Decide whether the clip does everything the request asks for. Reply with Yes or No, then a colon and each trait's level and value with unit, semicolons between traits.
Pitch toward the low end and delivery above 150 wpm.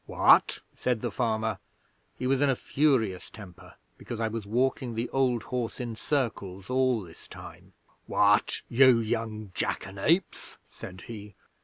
No: low, 115 Hz; average, 145 wpm